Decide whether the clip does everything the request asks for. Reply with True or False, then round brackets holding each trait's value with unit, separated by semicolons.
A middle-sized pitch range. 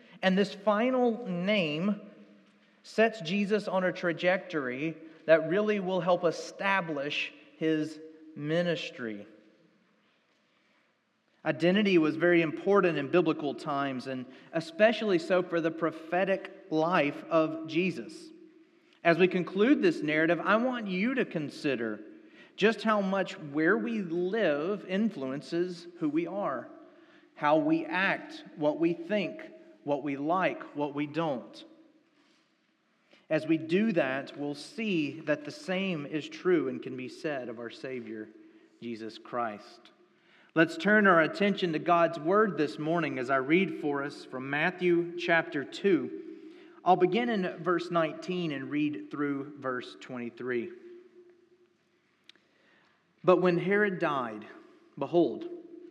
False (5.9 semitones)